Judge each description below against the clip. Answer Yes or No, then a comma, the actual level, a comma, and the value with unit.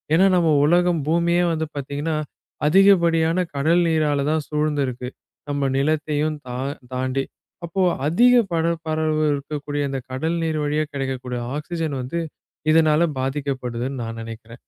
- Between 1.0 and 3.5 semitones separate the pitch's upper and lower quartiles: Yes, average, 3.2 semitones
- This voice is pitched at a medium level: Yes, medium, 150 Hz